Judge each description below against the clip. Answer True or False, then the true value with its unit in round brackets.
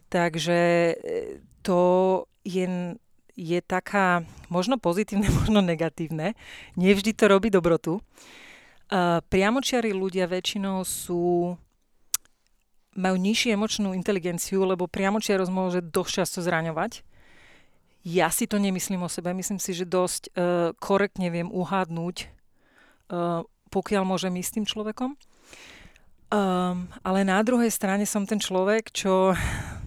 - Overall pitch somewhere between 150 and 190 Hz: True (185 Hz)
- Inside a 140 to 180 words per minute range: False (115 wpm)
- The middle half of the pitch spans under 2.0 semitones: False (2.4 semitones)